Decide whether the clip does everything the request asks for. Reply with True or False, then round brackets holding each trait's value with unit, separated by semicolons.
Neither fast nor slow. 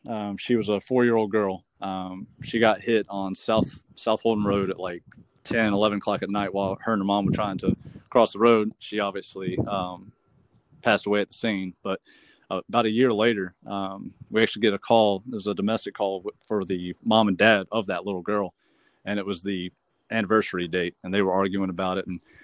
False (215 wpm)